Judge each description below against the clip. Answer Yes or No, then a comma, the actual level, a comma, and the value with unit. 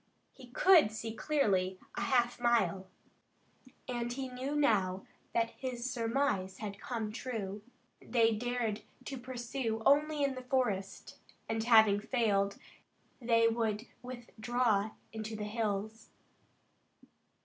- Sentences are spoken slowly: Yes, slow, 115 wpm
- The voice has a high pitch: Yes, high, 230 Hz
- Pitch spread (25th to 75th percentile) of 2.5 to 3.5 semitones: Yes, average, 2.9 semitones